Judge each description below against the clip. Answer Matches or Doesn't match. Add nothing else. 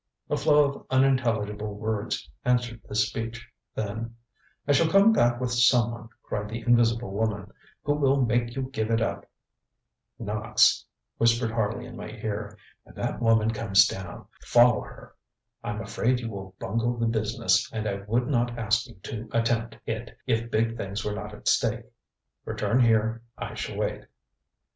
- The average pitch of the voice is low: Matches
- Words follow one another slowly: Doesn't match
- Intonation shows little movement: Matches